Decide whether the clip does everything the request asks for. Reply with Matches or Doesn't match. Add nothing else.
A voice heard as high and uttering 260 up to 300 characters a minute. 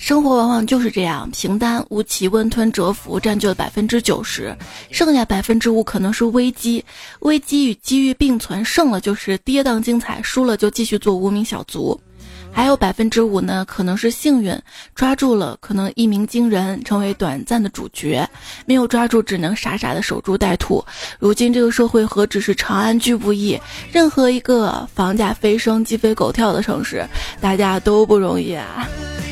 Matches